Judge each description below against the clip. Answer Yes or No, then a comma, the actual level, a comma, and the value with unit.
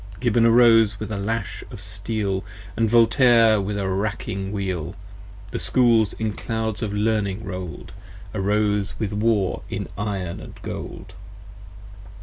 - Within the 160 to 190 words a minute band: No, slow, 135 wpm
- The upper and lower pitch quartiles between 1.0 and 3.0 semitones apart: Yes, narrow, 2.4 semitones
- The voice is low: Yes, low, 105 Hz